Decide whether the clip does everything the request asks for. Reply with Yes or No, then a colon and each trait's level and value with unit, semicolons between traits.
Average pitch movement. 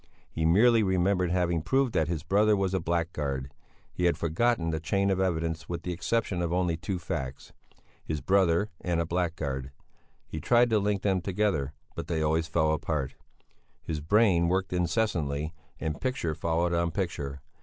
Yes: average, 3.3 semitones